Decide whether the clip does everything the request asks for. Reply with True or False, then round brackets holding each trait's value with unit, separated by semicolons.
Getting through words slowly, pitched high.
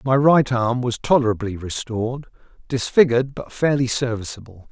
False (125 wpm; 125 Hz)